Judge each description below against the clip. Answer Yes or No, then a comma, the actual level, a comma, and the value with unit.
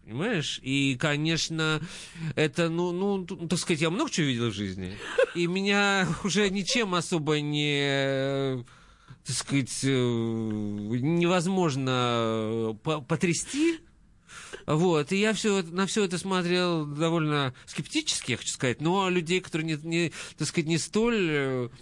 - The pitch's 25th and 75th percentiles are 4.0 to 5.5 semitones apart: Yes, average, 5.2 semitones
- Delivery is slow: No, average, 125 wpm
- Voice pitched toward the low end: No, medium, 160 Hz